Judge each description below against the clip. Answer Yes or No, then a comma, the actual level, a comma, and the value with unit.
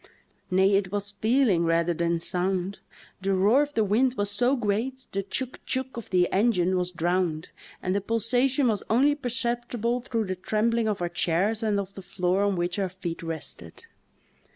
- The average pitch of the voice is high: Yes, high, 200 Hz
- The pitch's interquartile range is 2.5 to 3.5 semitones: No, average, 4.5 semitones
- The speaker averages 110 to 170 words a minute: No, average, 180 wpm